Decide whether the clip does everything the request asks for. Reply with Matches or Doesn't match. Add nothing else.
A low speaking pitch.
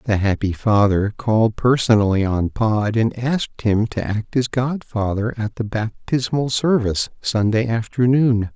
Matches